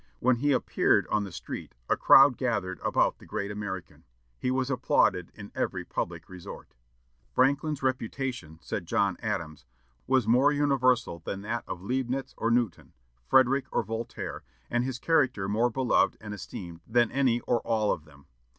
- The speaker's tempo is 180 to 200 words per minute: No, average, 160 wpm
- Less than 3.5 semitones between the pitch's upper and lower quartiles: No, average, 4.8 semitones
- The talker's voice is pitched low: Yes, low, 120 Hz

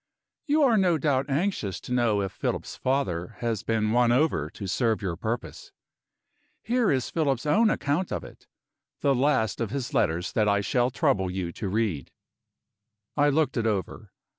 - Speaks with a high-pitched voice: No, low, 120 Hz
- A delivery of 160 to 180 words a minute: Yes, average, 170 wpm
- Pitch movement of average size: No, wide, 6.2 semitones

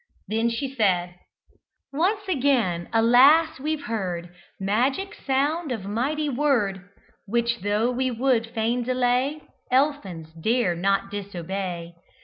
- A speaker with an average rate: No, slow, 115 wpm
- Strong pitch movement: Yes, wide, 5.7 semitones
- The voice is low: No, high, 235 Hz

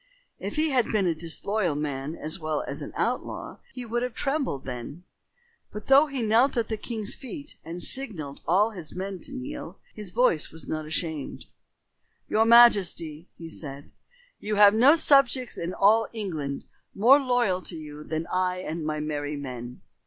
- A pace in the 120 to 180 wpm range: Yes, average, 175 wpm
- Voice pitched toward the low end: No, medium, 185 Hz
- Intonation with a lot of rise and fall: Yes, wide, 7.4 semitones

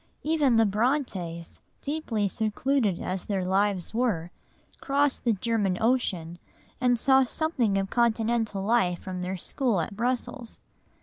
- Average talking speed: No, slow, 130 wpm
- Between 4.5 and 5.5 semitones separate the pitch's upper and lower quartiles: Yes, average, 4.8 semitones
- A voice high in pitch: Yes, high, 220 Hz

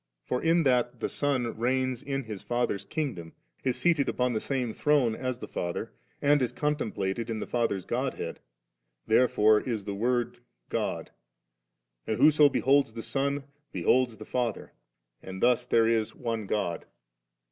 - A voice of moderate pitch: No, low, 120 Hz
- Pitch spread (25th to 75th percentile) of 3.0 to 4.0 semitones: Yes, average, 3.6 semitones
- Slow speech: No, average, 155 wpm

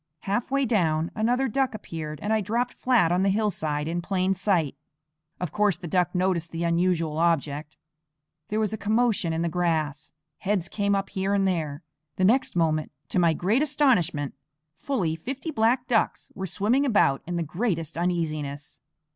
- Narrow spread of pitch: No, average, 4.9 semitones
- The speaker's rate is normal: Yes, average, 170 wpm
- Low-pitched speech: No, medium, 185 Hz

